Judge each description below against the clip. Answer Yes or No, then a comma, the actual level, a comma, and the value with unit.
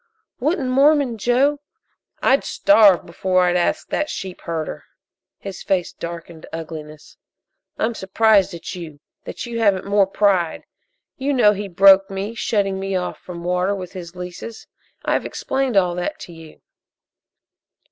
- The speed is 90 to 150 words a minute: Yes, average, 145 wpm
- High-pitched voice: Yes, high, 195 Hz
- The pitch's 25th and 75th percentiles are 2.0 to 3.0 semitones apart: No, average, 4.3 semitones